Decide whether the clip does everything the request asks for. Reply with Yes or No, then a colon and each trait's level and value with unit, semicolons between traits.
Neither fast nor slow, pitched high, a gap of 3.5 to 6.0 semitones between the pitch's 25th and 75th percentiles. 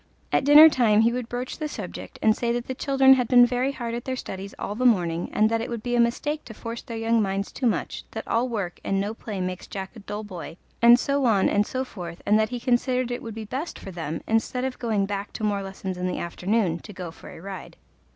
No: fast, 260 wpm; high, 225 Hz; average, 4.0 semitones